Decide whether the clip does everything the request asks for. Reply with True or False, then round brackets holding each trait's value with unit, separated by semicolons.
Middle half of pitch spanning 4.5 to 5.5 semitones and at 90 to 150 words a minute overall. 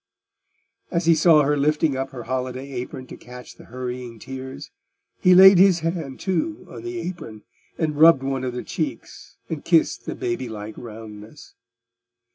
False (4.9 semitones; 165 wpm)